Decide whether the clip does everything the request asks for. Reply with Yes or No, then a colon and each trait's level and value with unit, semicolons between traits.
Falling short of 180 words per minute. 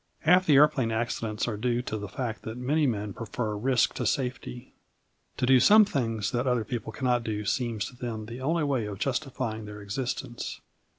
No: average, 190 wpm